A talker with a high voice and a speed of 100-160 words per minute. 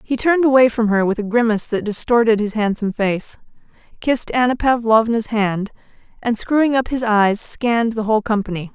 No: high, 225 Hz; average, 180 wpm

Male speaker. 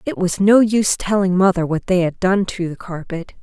No: female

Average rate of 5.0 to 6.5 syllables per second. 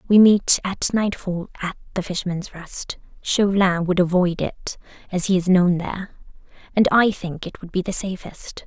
No: 4.8 syllables/s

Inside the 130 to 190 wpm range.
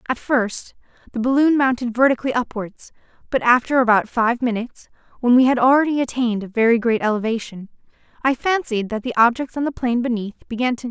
No: average, 200 wpm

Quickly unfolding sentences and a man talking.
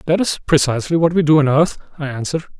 Yes: fast, 230 wpm; male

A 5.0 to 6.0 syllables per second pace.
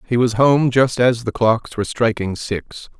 No: 4.4 syllables/s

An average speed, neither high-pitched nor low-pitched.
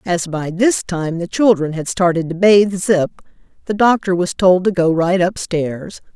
Yes: average, 185 wpm; medium, 180 Hz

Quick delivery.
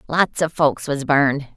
No: average, 190 wpm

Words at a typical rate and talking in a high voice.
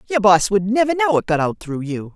No: fast, 280 wpm; high, 205 Hz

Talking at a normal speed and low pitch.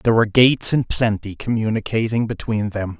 Yes: average, 160 wpm; low, 110 Hz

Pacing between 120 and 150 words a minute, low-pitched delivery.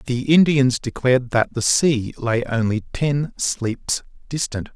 Yes: average, 140 wpm; low, 125 Hz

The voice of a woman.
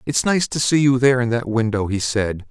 No: male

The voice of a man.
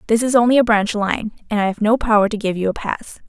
No: female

